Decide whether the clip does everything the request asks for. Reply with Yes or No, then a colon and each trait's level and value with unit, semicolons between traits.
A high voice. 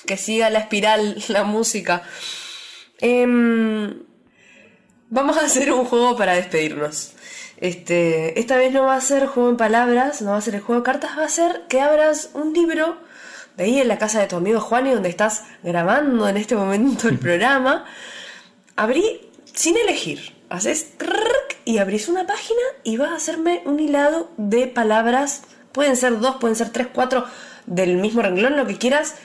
Yes: very high, 250 Hz